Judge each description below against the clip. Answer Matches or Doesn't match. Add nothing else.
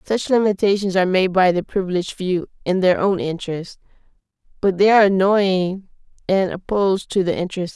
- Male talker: Doesn't match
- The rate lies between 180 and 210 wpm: Matches